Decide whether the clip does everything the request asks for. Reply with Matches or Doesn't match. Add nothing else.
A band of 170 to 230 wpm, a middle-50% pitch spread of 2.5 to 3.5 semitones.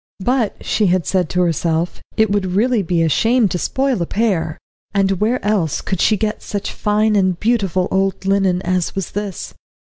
Matches